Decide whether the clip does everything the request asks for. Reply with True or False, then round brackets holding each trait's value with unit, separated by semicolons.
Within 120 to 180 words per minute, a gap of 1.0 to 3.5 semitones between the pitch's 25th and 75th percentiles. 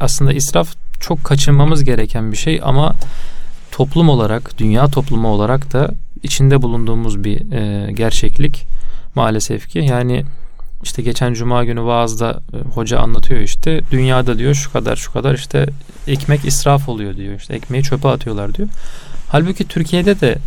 False (140 wpm; 4.0 semitones)